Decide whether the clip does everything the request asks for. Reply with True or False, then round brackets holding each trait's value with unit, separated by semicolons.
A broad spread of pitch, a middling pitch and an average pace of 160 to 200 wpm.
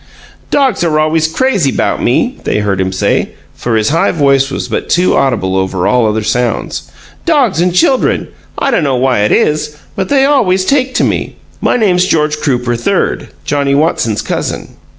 True (7.2 semitones; 150 Hz; 175 wpm)